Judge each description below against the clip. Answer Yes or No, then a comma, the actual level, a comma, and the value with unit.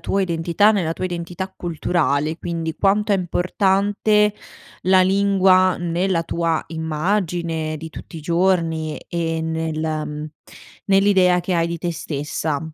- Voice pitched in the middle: Yes, medium, 170 Hz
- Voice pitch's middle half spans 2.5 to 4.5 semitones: Yes, average, 2.8 semitones